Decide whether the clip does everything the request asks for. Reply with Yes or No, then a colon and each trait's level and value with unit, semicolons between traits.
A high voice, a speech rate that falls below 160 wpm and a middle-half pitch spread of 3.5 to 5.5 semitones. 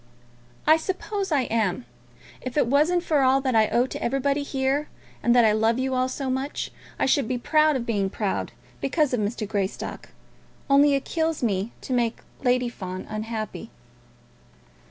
No: very high, 255 Hz; average, 175 wpm; average, 4.2 semitones